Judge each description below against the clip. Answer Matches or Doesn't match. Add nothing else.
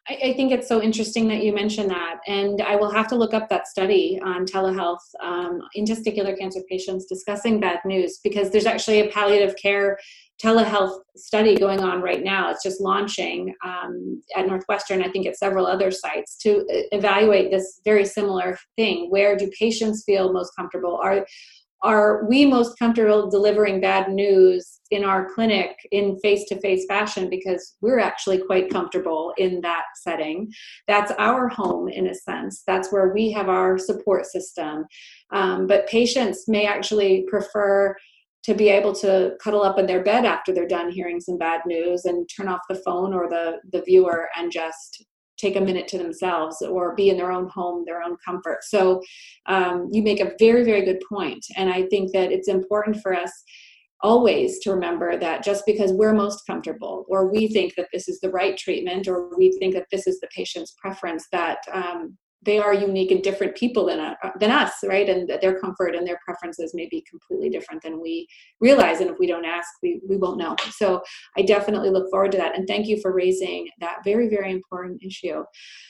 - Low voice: Doesn't match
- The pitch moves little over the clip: Matches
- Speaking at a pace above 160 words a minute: Matches